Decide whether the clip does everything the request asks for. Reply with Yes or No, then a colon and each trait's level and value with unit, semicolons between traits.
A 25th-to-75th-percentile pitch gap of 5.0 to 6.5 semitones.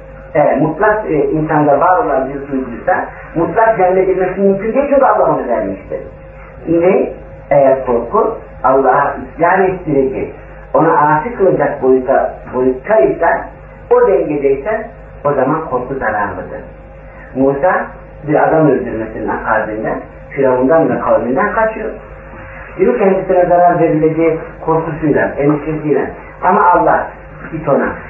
Yes: wide, 5.6 semitones